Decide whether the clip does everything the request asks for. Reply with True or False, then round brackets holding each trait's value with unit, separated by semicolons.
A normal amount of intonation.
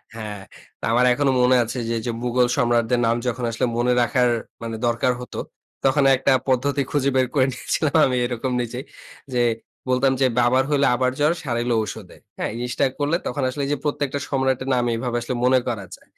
False (2.0 semitones)